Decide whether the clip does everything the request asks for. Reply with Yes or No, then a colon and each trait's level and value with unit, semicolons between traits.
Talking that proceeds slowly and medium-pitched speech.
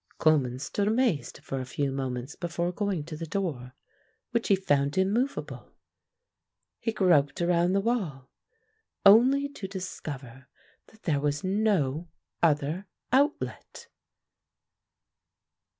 Yes: slow, 115 wpm; medium, 170 Hz